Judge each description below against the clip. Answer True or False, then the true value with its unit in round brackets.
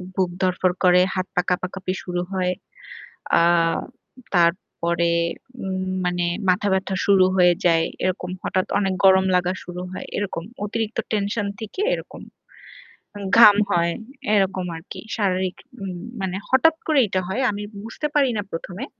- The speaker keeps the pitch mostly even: True (2.1 semitones)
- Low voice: False (185 Hz)